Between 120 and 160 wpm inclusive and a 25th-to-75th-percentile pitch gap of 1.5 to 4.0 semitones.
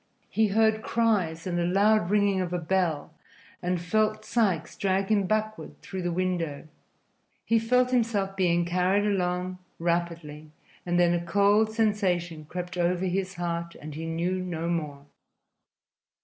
Yes: average, 150 wpm; average, 3.2 semitones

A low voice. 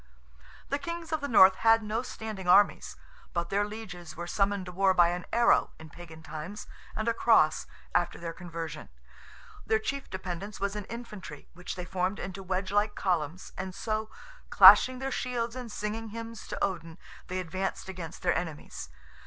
No: high, 190 Hz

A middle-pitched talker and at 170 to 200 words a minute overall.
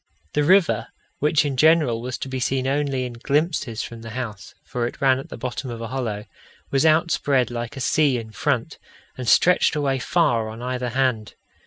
No: low, 130 Hz; average, 195 wpm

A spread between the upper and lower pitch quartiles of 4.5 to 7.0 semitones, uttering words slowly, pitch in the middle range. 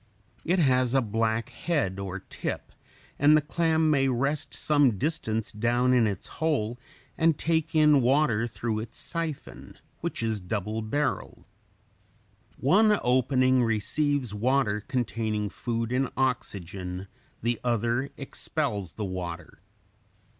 No: average, 5.0 semitones; slow, 130 wpm; low, 125 Hz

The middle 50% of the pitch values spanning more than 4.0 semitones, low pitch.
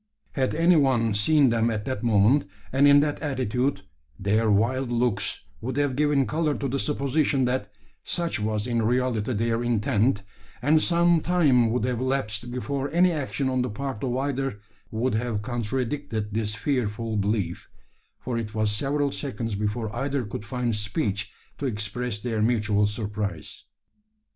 Yes: average, 4.4 semitones; low, 120 Hz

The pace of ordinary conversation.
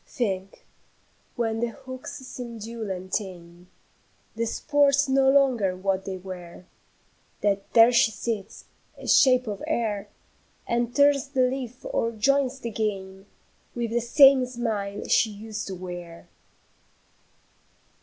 No: slow, 130 wpm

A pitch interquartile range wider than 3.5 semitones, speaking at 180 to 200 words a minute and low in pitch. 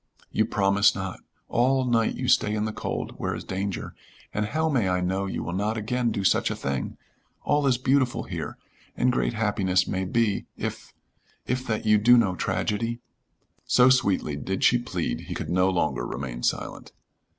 Yes: average, 4.5 semitones; average, 185 wpm; low, 105 Hz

